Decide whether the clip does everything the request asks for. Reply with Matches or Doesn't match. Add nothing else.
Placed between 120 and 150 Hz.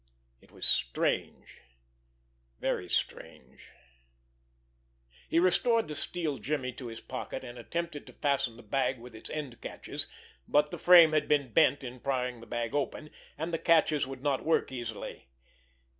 Matches